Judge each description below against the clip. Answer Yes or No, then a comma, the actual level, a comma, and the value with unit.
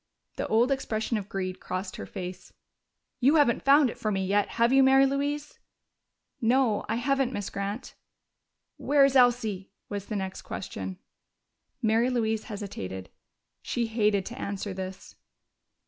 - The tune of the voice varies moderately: Yes, average, 4.8 semitones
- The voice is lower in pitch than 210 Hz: No, high, 220 Hz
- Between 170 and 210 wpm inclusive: No, average, 145 wpm